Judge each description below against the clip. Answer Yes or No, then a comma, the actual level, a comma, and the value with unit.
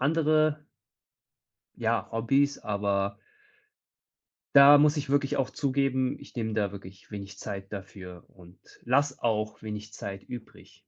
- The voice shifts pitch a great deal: Yes, wide, 5.8 semitones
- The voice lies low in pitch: Yes, low, 115 Hz